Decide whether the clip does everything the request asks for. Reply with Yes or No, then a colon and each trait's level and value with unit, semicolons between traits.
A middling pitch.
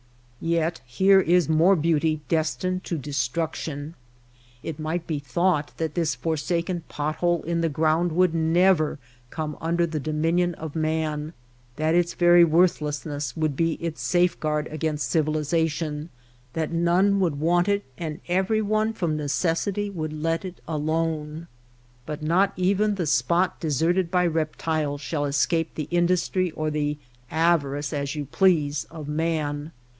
Yes: medium, 160 Hz